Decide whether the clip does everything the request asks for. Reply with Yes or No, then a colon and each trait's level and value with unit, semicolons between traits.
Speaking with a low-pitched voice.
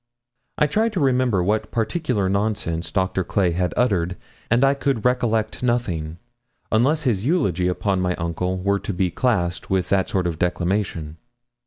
Yes: low, 100 Hz